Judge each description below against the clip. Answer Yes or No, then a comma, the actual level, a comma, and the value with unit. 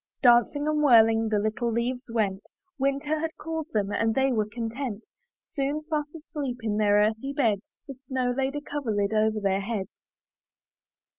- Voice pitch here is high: Yes, high, 240 Hz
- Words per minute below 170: Yes, average, 160 wpm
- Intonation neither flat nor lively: Yes, average, 4.5 semitones